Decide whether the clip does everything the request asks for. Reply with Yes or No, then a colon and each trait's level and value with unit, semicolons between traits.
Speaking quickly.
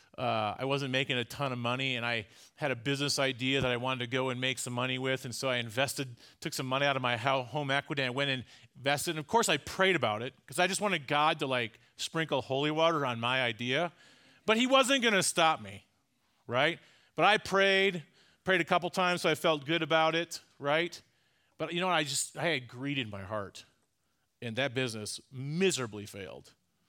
Yes: fast, 225 wpm